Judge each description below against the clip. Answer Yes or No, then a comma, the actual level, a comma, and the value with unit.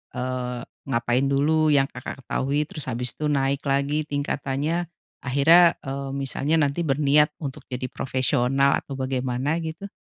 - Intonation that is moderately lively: No, narrow, 2.2 semitones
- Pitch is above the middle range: No, medium, 140 Hz